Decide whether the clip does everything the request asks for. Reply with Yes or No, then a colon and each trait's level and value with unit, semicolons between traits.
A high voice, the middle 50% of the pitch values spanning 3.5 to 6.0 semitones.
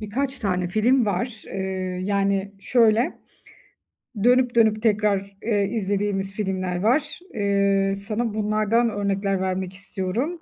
No: high, 205 Hz; average, 2.7 semitones